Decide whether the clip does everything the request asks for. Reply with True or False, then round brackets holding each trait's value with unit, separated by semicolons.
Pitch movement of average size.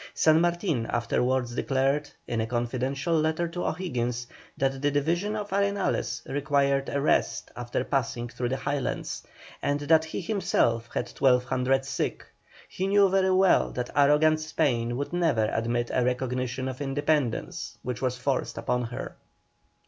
True (4.2 semitones)